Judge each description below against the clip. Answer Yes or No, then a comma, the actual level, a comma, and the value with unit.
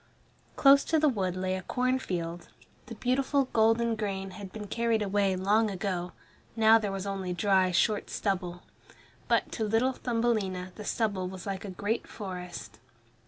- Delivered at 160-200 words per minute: Yes, average, 165 wpm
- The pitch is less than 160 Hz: No, high, 205 Hz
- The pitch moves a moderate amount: Yes, average, 3.4 semitones